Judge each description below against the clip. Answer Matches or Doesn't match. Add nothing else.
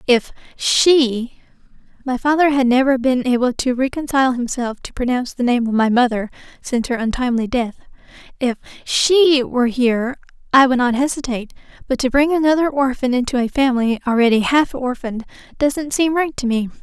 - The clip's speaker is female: Matches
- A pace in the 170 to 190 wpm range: Doesn't match